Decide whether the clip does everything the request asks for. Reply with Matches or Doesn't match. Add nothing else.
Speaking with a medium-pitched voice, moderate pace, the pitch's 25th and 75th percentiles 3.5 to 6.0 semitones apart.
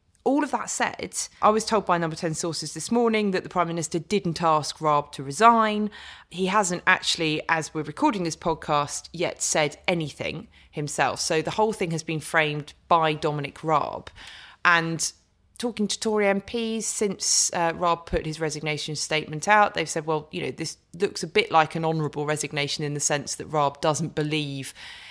Matches